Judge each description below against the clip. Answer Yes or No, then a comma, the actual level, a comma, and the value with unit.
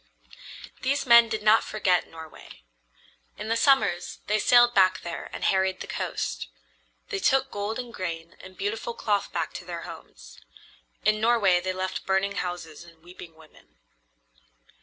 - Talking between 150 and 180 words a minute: Yes, average, 155 wpm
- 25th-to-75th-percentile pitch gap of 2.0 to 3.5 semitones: No, average, 4.3 semitones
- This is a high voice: Yes, high, 195 Hz